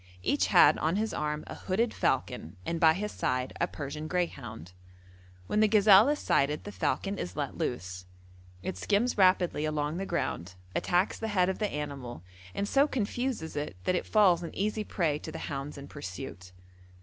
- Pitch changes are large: Yes, wide, 6.5 semitones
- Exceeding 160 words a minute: Yes, average, 185 wpm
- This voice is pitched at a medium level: Yes, medium, 165 Hz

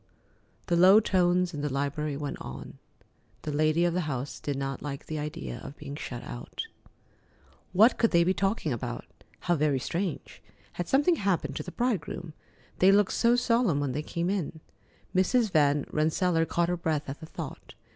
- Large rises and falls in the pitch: No, average, 4.4 semitones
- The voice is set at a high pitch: No, medium, 165 Hz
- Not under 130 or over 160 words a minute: No, average, 180 wpm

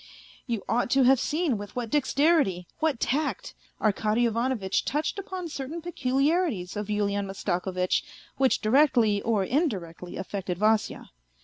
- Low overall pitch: No, high, 235 Hz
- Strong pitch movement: Yes, wide, 6.3 semitones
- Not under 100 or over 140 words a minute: Yes, slow, 135 wpm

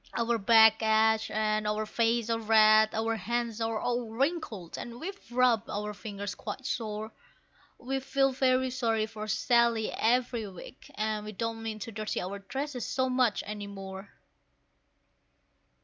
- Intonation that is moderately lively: No, narrow, 2.1 semitones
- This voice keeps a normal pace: Yes, average, 150 wpm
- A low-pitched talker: No, high, 225 Hz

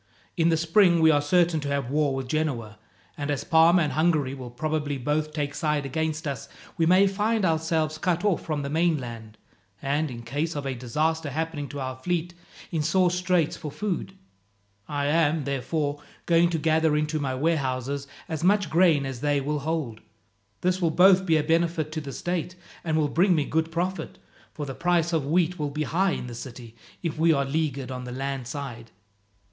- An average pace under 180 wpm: No, average, 195 wpm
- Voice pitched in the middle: Yes, medium, 155 Hz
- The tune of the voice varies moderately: Yes, average, 3.1 semitones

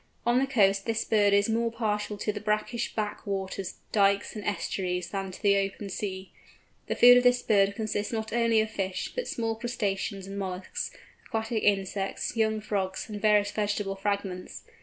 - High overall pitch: Yes, high, 205 Hz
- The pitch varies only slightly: Yes, narrow, 2.1 semitones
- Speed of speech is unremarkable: Yes, average, 180 wpm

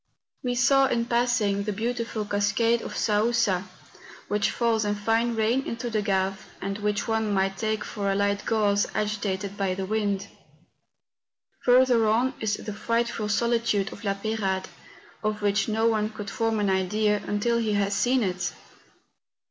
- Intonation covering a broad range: No, narrow, 2.4 semitones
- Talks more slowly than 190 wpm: Yes, average, 160 wpm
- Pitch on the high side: Yes, high, 215 Hz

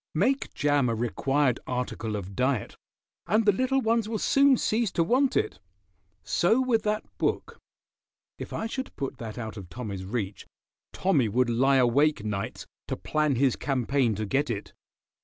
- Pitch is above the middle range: No, low, 135 Hz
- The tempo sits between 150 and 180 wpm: Yes, average, 165 wpm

